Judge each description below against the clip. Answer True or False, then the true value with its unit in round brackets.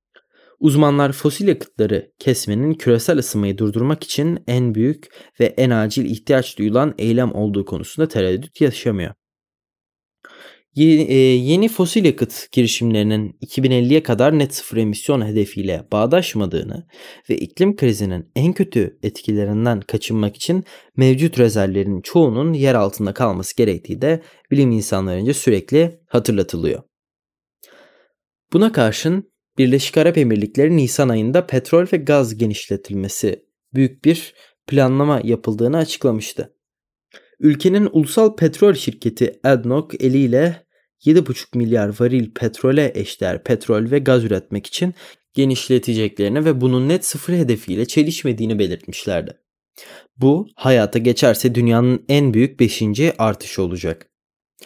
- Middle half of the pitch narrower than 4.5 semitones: False (5.5 semitones)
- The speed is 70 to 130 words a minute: True (110 wpm)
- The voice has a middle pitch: False (130 Hz)